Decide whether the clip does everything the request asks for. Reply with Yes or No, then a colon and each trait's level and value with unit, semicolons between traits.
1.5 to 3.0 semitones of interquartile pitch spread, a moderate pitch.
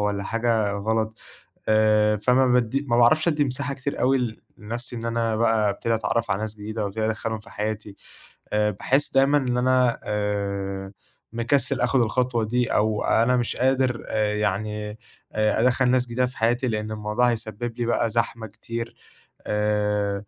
No: average, 2.7 semitones; low, 115 Hz